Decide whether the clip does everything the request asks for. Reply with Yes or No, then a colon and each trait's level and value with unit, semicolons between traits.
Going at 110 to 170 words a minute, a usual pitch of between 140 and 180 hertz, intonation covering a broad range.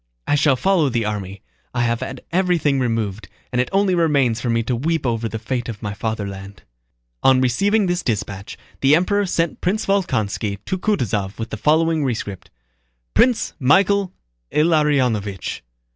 No: average, 160 wpm; low, 130 Hz; wide, 7.4 semitones